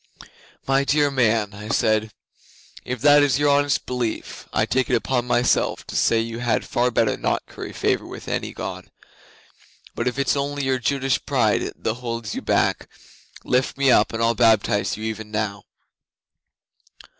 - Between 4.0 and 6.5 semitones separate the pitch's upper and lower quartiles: No, average, 3.4 semitones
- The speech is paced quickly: No, average, 170 wpm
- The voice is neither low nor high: No, low, 120 Hz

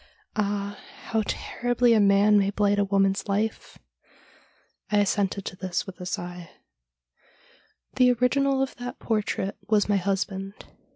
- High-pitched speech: Yes, high, 205 Hz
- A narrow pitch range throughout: Yes, narrow, 2.3 semitones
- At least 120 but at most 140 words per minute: No, average, 150 wpm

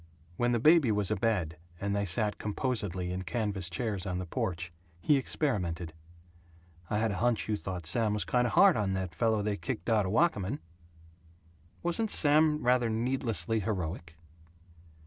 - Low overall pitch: Yes, low, 105 Hz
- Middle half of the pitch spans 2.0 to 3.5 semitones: No, average, 4.7 semitones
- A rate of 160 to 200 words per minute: Yes, average, 165 wpm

